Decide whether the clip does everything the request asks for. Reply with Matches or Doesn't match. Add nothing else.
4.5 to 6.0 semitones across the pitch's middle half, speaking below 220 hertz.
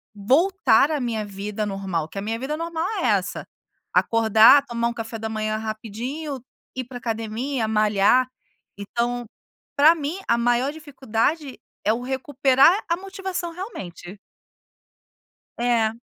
Doesn't match